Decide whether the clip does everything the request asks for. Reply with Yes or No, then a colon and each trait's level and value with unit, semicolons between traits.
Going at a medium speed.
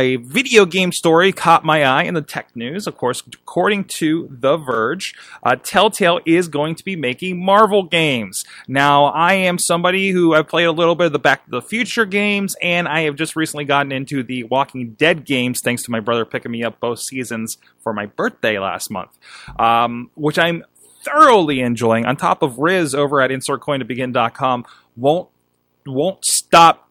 Yes: average, 185 wpm